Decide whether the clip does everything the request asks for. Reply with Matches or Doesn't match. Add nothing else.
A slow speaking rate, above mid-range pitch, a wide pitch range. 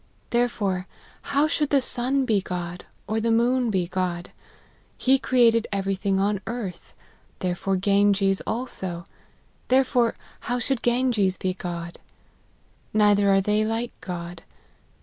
Doesn't match